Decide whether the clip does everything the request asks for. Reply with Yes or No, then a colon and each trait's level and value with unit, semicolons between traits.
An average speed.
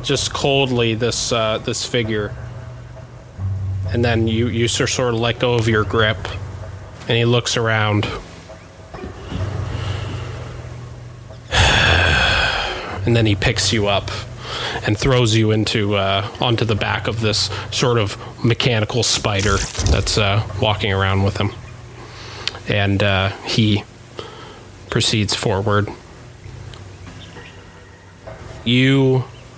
No: slow, 110 wpm